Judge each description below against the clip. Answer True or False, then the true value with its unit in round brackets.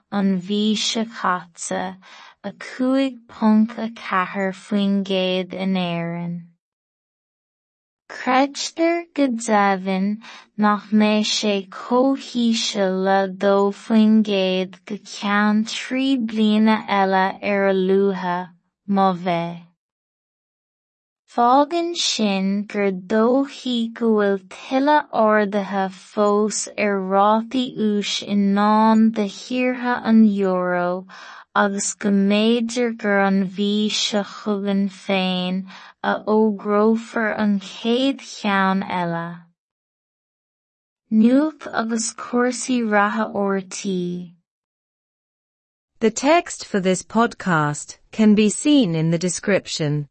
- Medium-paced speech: False (85 wpm)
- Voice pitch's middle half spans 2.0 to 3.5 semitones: True (2.9 semitones)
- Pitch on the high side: True (205 Hz)